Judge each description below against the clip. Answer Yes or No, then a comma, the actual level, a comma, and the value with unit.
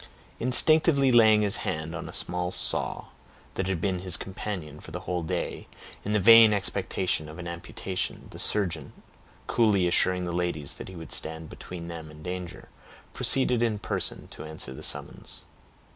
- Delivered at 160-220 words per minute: Yes, average, 170 wpm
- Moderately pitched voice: No, very low, 90 Hz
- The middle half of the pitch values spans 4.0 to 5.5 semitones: Yes, average, 4.3 semitones